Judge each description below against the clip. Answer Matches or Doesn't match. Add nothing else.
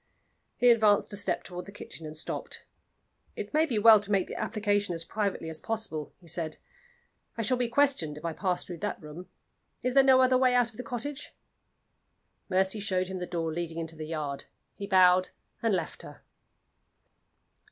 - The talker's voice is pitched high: Matches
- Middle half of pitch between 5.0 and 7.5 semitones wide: Matches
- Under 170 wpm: Doesn't match